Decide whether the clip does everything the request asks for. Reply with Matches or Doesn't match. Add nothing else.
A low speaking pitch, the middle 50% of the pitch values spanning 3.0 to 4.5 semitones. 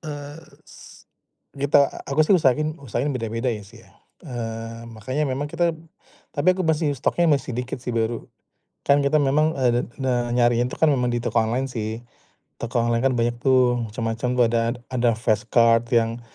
Matches